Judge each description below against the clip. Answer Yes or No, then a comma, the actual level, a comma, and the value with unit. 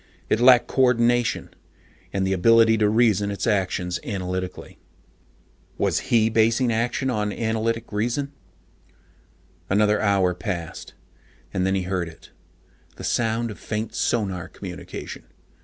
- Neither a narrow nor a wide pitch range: Yes, average, 3.4 semitones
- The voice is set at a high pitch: No, low, 110 Hz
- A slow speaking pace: Yes, slow, 125 wpm